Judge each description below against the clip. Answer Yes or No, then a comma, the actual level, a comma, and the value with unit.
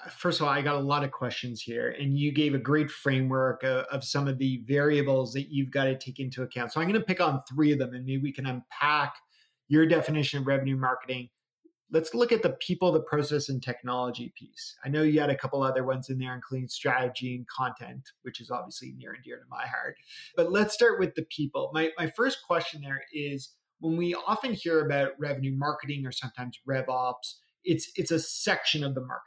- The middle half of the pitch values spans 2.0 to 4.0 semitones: Yes, average, 3.5 semitones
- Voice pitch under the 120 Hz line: No, medium, 140 Hz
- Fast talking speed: Yes, fast, 230 wpm